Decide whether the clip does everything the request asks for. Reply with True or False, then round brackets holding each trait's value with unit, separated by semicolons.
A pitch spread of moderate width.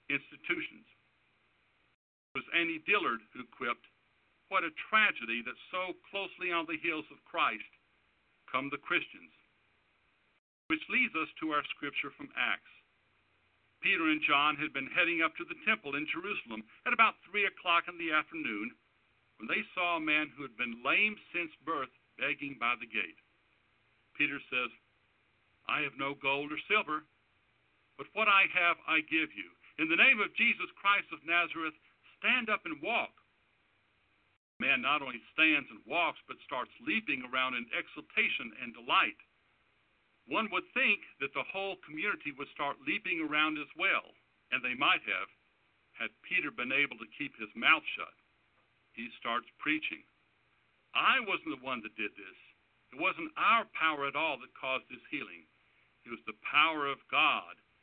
False (5.9 semitones)